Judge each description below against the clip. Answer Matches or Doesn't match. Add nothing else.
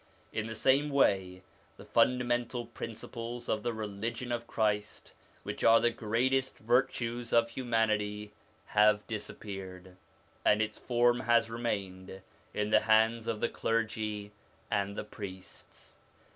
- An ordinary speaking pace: Doesn't match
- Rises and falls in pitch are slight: Matches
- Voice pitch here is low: Matches